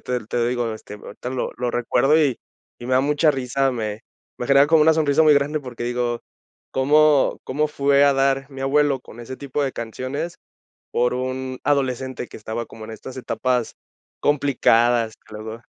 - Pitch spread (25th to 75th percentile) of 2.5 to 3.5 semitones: Yes, average, 2.9 semitones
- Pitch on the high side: No, low, 130 Hz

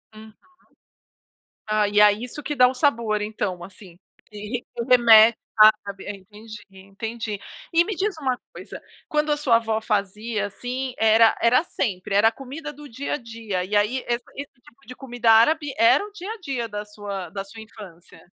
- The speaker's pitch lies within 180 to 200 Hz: No, high, 225 Hz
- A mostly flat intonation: No, average, 3.9 semitones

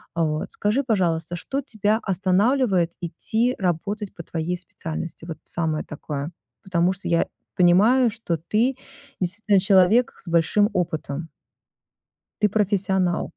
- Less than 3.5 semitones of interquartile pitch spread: No, average, 4.0 semitones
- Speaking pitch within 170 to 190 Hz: Yes, medium, 185 Hz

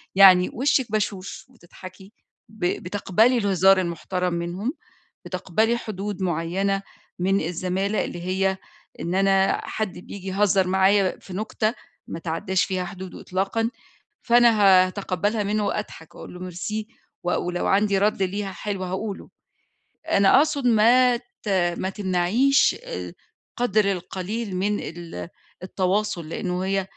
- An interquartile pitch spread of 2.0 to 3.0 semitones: Yes, narrow, 2.6 semitones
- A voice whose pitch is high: Yes, high, 195 Hz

